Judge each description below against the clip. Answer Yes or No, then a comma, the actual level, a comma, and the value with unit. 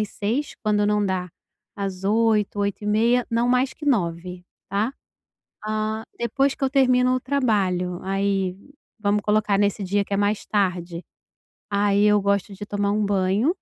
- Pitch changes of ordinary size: No, narrow, 2.3 semitones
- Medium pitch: No, high, 205 Hz